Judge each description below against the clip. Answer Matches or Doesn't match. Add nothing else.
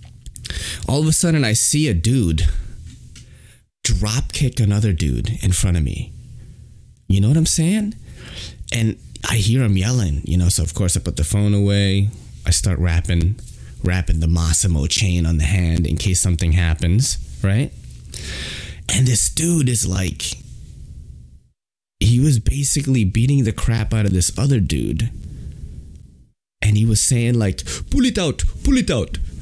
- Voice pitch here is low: Matches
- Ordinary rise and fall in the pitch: Doesn't match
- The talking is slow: Doesn't match